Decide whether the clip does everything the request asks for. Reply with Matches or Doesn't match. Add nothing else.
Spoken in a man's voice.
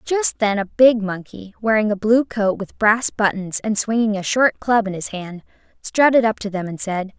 Doesn't match